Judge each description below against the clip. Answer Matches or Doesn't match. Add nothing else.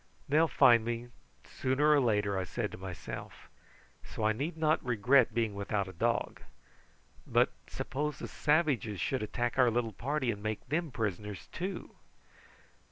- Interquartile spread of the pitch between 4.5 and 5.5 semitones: Matches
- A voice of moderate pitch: Doesn't match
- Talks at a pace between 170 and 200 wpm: Doesn't match